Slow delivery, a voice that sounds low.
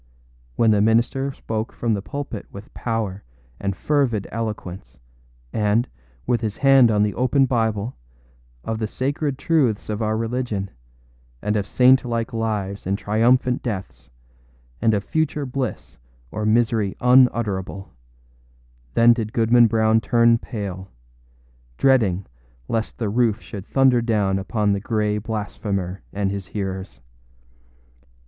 Yes: slow, 130 wpm; low, 110 Hz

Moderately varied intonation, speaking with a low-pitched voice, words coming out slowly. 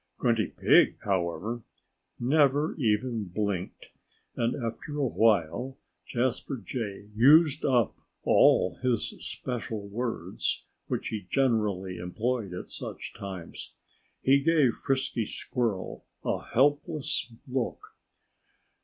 Yes: average, 4.5 semitones; low, 115 Hz; slow, 100 wpm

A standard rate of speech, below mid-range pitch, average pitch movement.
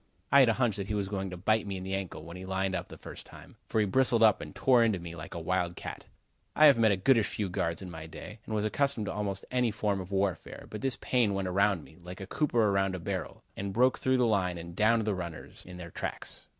No: fast, 275 wpm; low, 100 Hz; average, 3.3 semitones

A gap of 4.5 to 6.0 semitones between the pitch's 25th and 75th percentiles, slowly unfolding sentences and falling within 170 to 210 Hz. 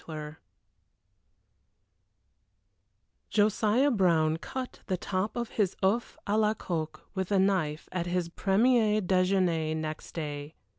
Yes: average, 4.8 semitones; slow, 115 wpm; medium, 185 Hz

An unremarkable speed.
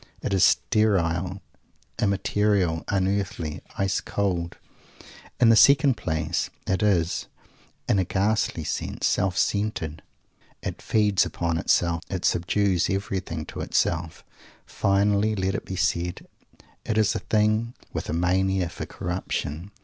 No: slow, 125 wpm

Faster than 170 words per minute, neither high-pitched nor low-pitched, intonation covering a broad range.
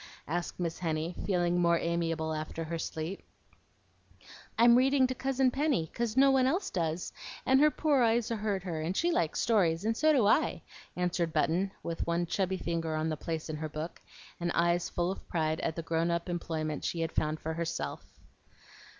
Yes: average, 190 wpm; medium, 175 Hz; wide, 5.7 semitones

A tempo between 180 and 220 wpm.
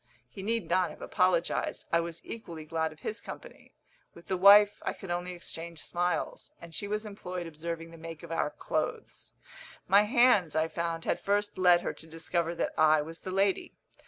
Yes: average, 190 wpm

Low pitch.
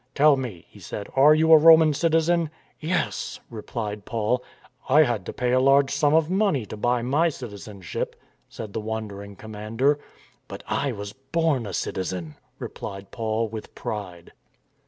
Yes: low, 125 Hz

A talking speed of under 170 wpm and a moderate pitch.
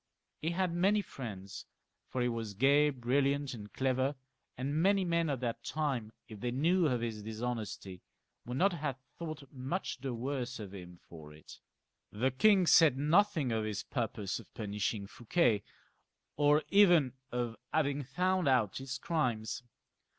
No: average, 155 wpm; low, 130 Hz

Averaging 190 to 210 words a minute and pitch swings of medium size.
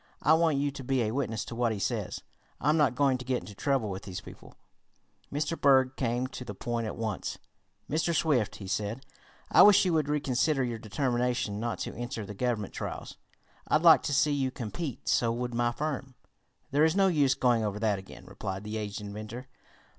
Yes: fast, 205 wpm; average, 4.5 semitones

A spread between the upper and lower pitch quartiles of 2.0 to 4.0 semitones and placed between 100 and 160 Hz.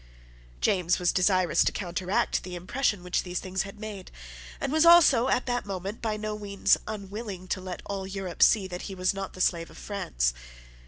No: narrow, 2.6 semitones; high, 195 Hz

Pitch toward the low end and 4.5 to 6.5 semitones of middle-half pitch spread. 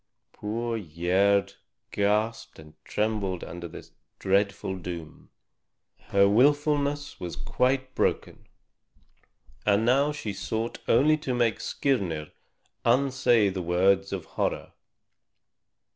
Yes: low, 105 Hz; average, 5.2 semitones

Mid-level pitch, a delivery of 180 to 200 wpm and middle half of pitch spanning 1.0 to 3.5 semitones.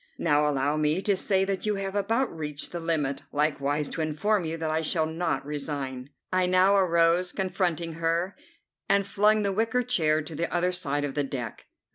No: medium, 165 Hz; average, 190 wpm; average, 4.3 semitones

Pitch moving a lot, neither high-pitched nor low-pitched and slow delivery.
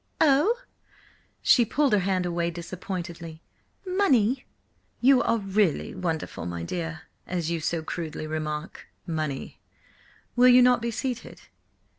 Yes: wide, 7.1 semitones; medium, 180 Hz; slow, 120 wpm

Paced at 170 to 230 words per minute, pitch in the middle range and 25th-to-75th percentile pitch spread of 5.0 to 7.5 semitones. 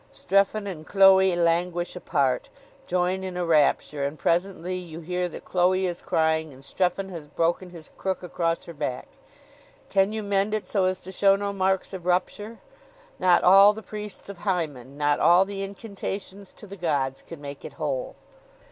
No: average, 175 wpm; medium, 180 Hz; average, 2.9 semitones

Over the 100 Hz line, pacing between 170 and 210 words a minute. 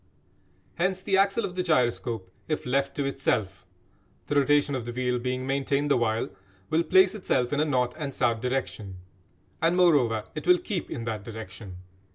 Yes: low, 135 Hz; average, 180 wpm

